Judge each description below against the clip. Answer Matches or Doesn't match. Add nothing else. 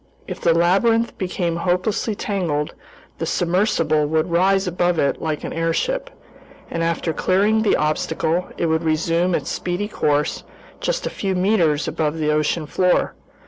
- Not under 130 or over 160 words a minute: Matches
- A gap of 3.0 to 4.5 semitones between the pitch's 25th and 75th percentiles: Matches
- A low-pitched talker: Doesn't match